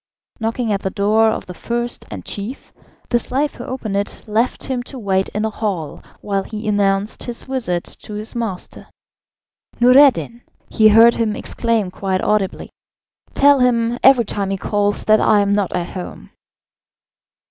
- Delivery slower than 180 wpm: Yes, average, 165 wpm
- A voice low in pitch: No, high, 215 Hz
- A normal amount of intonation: Yes, average, 3.0 semitones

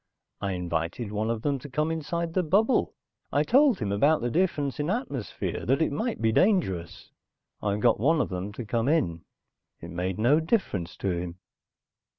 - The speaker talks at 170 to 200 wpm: Yes, average, 180 wpm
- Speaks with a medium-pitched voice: No, low, 120 Hz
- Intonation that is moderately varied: No, wide, 8.6 semitones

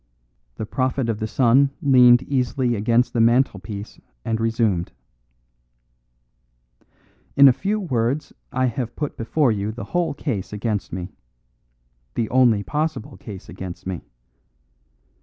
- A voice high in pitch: No, low, 120 Hz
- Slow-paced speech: Yes, slow, 125 wpm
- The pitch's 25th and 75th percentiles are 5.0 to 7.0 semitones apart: No, average, 3.7 semitones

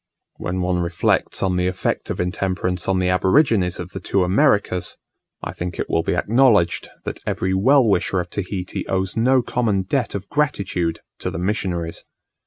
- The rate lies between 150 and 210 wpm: Yes, average, 175 wpm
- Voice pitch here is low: Yes, very low, 95 Hz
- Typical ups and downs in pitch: Yes, average, 3.0 semitones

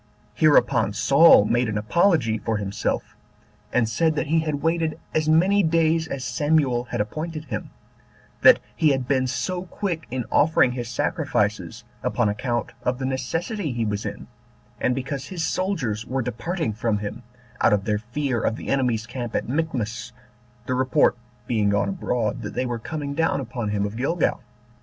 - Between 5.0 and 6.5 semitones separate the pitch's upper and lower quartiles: Yes, wide, 5.6 semitones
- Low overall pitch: Yes, low, 130 Hz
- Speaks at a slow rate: No, average, 170 wpm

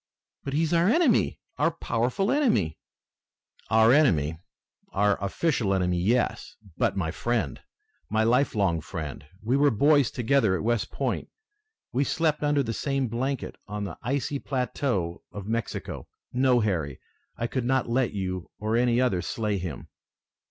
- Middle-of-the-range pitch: No, low, 115 Hz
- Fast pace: No, average, 150 wpm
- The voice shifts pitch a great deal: Yes, wide, 5.9 semitones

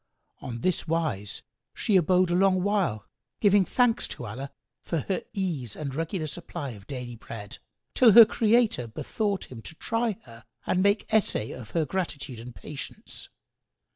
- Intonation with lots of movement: Yes, wide, 8.2 semitones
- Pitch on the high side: No, medium, 165 Hz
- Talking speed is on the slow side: No, average, 165 wpm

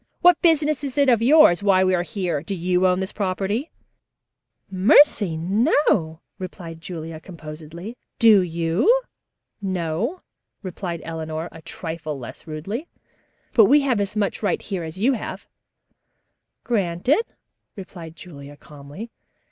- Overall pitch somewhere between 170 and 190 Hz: Yes, medium, 185 Hz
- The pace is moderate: No, slow, 130 wpm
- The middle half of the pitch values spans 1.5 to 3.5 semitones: No, wide, 5.6 semitones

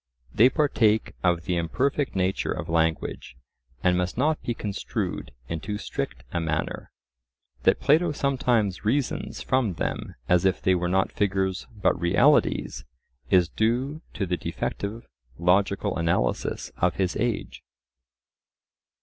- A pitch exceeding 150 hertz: No, very low, 95 Hz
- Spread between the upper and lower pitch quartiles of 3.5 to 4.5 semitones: No, average, 5.0 semitones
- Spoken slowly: Yes, slow, 130 wpm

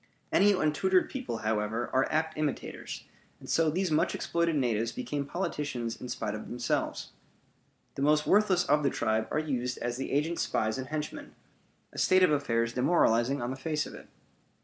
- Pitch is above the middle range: No, medium, 145 Hz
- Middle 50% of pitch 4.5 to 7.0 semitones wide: Yes, average, 4.9 semitones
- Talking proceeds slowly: No, average, 175 wpm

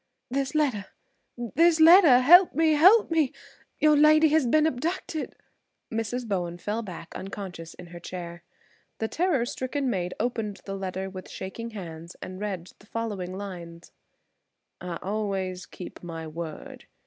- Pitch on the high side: Yes, high, 210 Hz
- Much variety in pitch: Yes, wide, 8.1 semitones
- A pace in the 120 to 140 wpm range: Yes, slow, 135 wpm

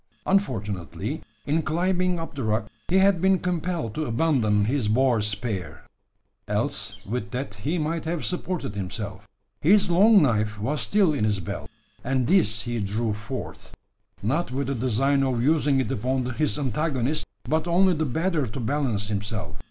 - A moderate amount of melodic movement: No, wide, 7.2 semitones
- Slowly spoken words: No, average, 160 wpm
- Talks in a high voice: No, low, 135 Hz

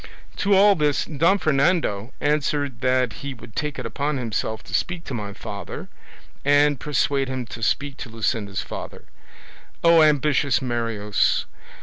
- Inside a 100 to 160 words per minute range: Yes, average, 145 wpm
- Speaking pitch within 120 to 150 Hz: Yes, medium, 140 Hz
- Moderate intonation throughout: Yes, average, 4.5 semitones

